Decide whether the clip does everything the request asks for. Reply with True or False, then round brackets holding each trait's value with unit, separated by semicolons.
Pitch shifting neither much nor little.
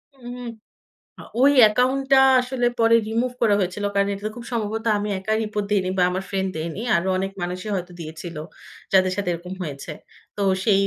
True (3.6 semitones)